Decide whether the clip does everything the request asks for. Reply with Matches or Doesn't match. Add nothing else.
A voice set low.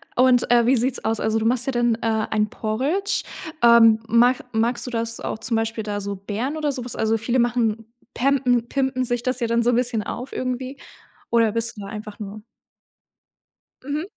Doesn't match